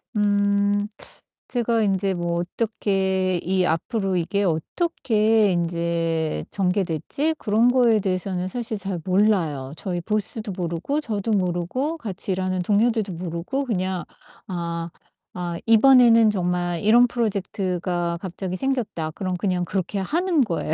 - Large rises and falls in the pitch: No, average, 3.8 semitones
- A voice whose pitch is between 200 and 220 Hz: No, high, 190 Hz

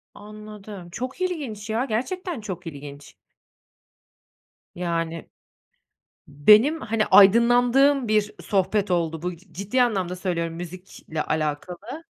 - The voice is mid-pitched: No, high, 205 Hz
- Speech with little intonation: No, wide, 5.4 semitones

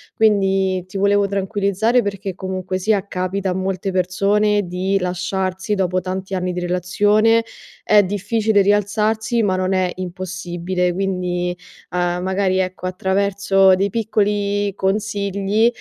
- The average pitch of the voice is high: Yes, high, 195 Hz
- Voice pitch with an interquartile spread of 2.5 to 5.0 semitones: No, narrow, 1.8 semitones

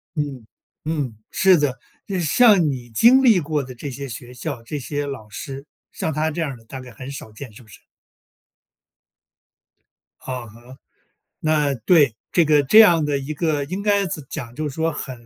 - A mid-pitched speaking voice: Yes, medium, 145 Hz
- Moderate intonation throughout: Yes, average, 4.0 semitones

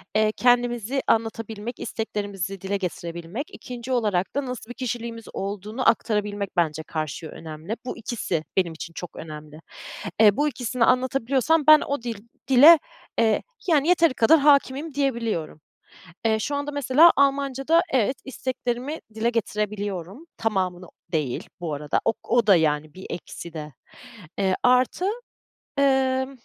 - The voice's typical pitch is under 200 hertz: No, high, 225 Hz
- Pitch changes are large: Yes, wide, 5.8 semitones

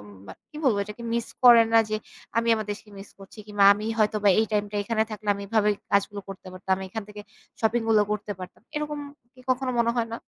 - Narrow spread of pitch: Yes, narrow, 2.2 semitones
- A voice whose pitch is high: Yes, high, 215 Hz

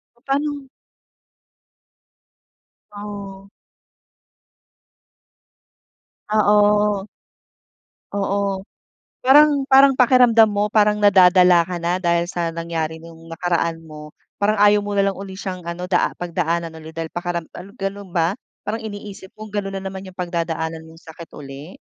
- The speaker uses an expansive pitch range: No, average, 3.5 semitones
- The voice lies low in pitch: No, high, 190 Hz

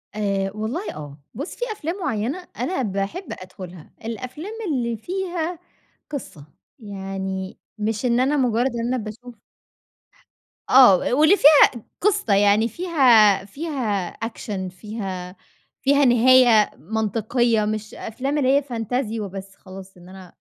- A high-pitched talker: Yes, high, 225 Hz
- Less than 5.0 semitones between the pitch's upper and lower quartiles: No, average, 5.3 semitones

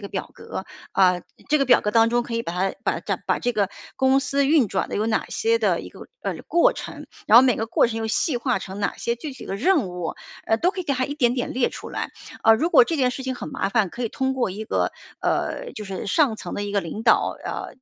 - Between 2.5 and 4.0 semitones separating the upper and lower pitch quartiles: No, average, 4.6 semitones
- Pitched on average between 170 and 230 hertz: No, high, 240 Hz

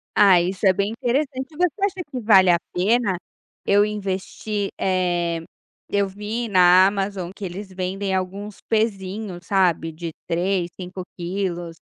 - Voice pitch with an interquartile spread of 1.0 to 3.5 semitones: Yes, narrow, 2.5 semitones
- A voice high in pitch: Yes, high, 195 Hz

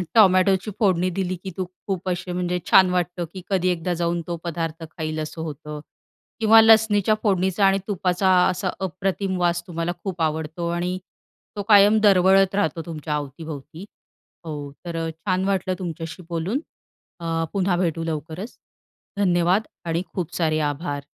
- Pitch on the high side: No, medium, 180 Hz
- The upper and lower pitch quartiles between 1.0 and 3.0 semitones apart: Yes, average, 2.7 semitones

